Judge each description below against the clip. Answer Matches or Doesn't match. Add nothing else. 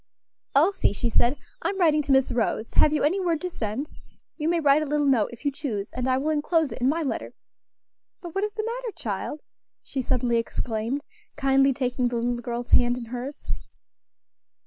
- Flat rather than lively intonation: Doesn't match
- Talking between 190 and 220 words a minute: Matches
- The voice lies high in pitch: Matches